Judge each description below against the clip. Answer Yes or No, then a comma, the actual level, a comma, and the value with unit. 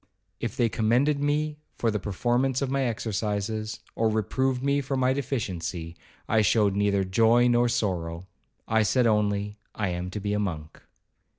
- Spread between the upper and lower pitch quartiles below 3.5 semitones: No, average, 3.8 semitones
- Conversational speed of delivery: Yes, average, 160 wpm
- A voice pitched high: No, low, 110 Hz